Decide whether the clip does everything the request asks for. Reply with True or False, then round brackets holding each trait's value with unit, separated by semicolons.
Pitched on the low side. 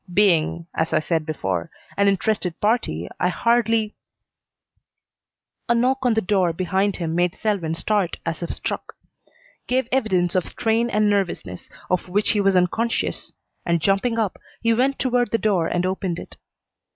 False (195 Hz)